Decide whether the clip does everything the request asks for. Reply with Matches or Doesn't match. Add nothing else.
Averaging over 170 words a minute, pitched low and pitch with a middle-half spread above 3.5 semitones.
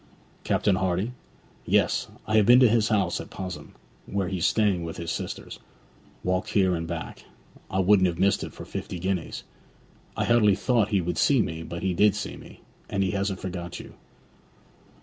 Doesn't match